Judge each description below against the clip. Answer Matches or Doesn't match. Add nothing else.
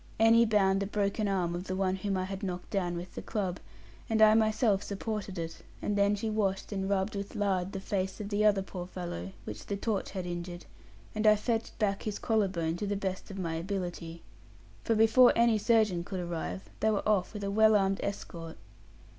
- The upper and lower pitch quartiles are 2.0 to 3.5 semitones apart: Matches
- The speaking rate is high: Matches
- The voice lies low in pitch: Doesn't match